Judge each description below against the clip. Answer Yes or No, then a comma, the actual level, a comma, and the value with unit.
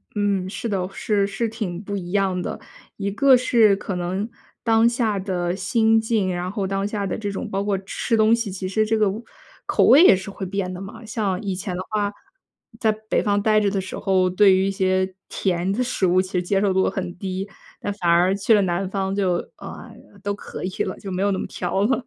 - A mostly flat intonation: Yes, narrow, 2.3 semitones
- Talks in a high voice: Yes, high, 195 Hz